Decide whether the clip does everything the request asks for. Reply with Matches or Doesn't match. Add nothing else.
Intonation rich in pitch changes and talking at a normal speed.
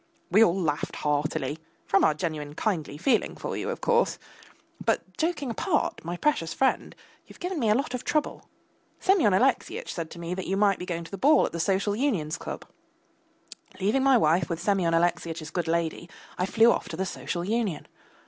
Matches